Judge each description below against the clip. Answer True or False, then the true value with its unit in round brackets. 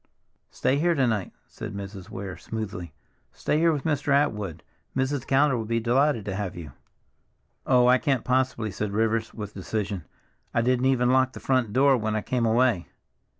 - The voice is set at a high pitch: False (115 Hz)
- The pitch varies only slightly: False (4.1 semitones)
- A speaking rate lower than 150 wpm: False (180 wpm)